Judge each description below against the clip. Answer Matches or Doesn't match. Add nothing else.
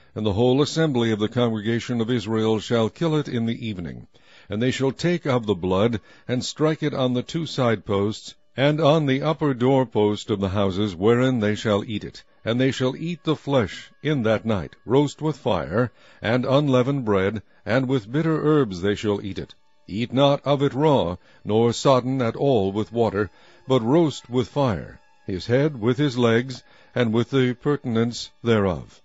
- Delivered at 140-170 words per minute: Doesn't match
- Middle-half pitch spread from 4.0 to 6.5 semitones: Matches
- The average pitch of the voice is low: Matches